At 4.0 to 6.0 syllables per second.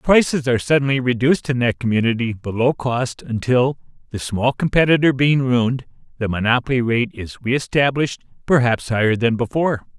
Yes: 5.5 syllables/s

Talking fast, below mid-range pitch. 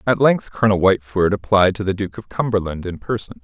Yes: fast, 210 wpm; low, 100 Hz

